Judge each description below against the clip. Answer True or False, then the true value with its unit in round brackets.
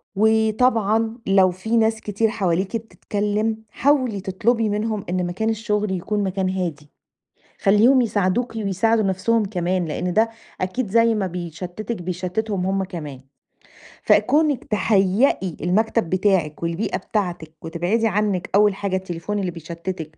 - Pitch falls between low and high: False (200 Hz)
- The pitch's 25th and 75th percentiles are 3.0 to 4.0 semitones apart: True (3.4 semitones)